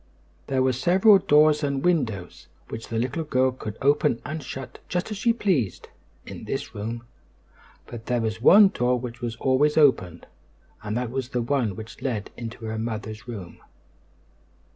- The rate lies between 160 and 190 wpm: Yes, average, 165 wpm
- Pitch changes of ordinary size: Yes, average, 4.8 semitones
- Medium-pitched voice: No, low, 125 Hz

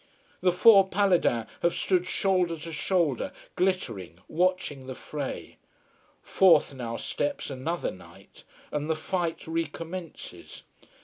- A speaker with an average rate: No, slow, 115 wpm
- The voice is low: No, medium, 165 Hz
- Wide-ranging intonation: No, average, 4.1 semitones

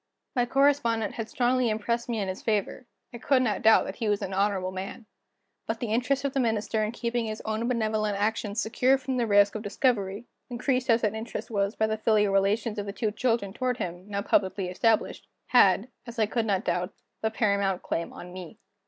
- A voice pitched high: Yes, high, 220 Hz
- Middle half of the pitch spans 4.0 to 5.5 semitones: No, average, 2.9 semitones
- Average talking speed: No, fast, 210 wpm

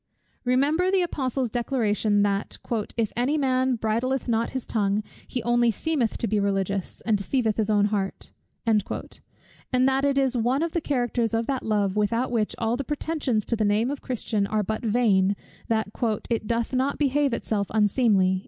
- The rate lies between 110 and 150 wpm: No, average, 170 wpm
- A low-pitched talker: No, high, 230 Hz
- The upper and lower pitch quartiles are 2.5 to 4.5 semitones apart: Yes, average, 3.7 semitones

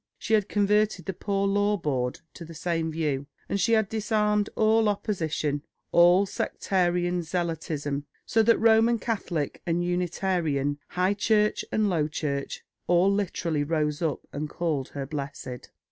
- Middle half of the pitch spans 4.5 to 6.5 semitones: Yes, average, 5.3 semitones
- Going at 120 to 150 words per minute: Yes, average, 145 wpm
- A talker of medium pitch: Yes, medium, 175 Hz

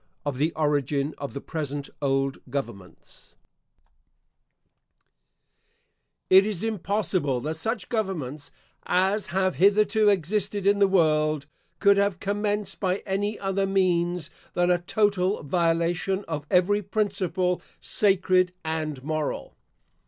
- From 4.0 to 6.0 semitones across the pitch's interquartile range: Yes, average, 4.6 semitones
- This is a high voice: No, medium, 180 Hz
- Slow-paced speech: Yes, slow, 115 wpm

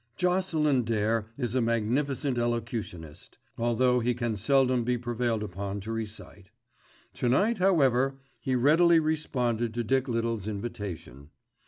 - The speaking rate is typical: No, slow, 130 wpm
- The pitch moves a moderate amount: Yes, average, 3.4 semitones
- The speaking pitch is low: Yes, low, 120 Hz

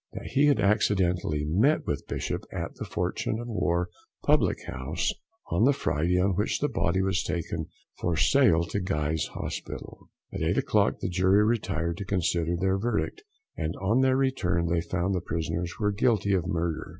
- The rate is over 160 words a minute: Yes, average, 175 wpm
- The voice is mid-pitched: No, very low, 90 Hz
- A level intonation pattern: No, average, 3.8 semitones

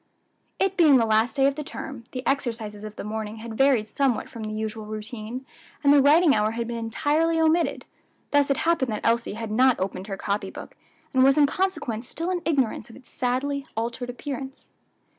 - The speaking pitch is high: Yes, very high, 250 Hz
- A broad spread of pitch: No, average, 4.5 semitones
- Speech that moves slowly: No, average, 200 wpm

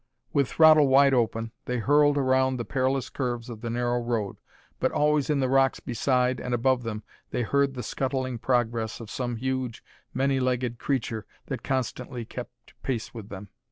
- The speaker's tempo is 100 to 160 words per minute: No, average, 175 wpm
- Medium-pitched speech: No, low, 125 Hz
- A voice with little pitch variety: Yes, narrow, 2.2 semitones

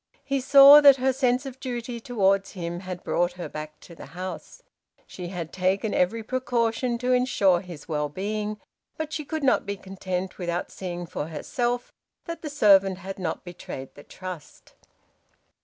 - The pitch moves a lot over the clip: Yes, wide, 5.9 semitones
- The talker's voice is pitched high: Yes, high, 195 Hz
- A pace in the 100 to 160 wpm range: No, average, 170 wpm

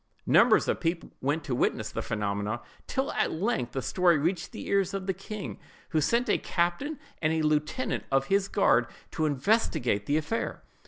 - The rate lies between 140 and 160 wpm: No, average, 180 wpm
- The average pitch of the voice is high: No, medium, 165 Hz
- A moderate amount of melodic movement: No, wide, 5.7 semitones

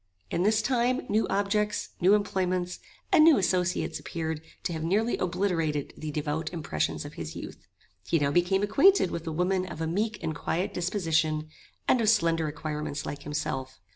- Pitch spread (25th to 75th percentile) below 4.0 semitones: No, average, 4.6 semitones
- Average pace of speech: Yes, average, 170 wpm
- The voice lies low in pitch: No, medium, 175 Hz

